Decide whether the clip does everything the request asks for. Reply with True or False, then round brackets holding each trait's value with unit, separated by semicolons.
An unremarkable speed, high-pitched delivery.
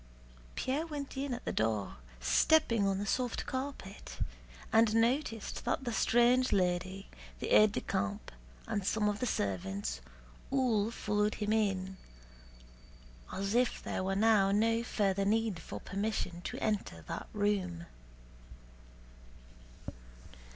False (130 wpm; 210 Hz)